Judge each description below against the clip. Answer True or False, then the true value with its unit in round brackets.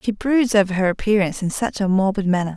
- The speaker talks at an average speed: False (235 wpm)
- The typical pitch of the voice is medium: False (200 Hz)